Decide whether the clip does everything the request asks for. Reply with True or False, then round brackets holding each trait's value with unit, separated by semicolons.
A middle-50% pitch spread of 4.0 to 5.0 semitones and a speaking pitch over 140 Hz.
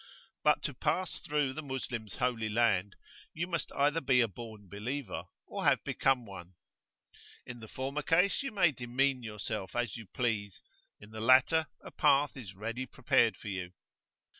False (4.6 semitones; 120 Hz)